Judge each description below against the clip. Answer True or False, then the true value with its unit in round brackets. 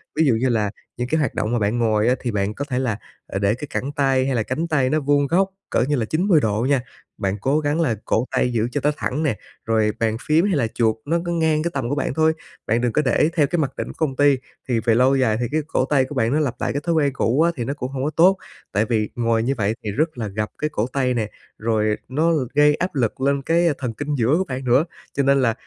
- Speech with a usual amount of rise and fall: True (4.6 semitones)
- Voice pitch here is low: True (130 Hz)